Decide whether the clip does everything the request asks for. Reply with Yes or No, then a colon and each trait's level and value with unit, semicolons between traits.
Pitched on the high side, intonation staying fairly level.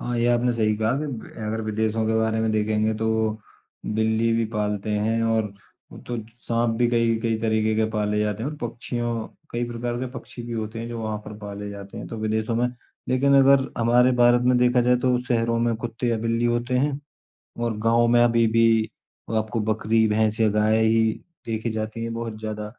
No: low, 115 Hz; narrow, 1.4 semitones